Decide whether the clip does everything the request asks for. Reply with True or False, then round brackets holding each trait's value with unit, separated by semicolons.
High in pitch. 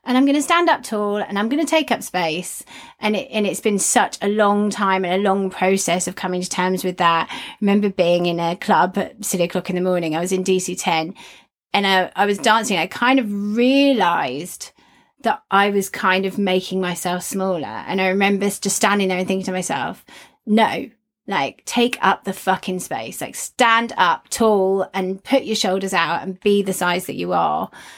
True (195 Hz)